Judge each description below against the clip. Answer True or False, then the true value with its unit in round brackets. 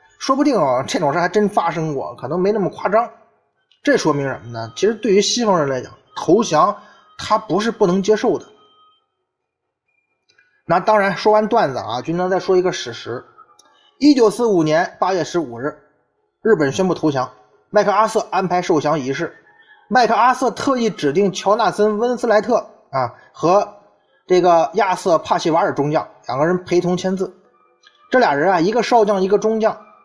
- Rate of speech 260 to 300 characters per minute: True (265 characters per minute)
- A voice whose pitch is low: False (205 Hz)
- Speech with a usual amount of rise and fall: True (4.9 semitones)